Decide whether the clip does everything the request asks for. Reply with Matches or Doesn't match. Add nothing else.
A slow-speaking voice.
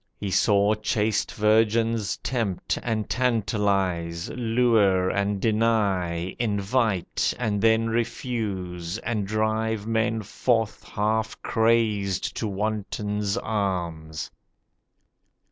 Matches